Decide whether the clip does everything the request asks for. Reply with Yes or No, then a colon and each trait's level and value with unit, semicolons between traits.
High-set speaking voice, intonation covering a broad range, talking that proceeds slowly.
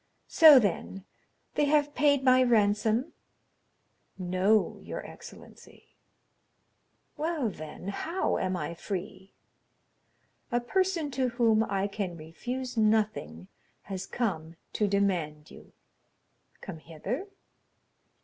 Yes: high, 215 Hz; wide, 5.8 semitones; slow, 100 wpm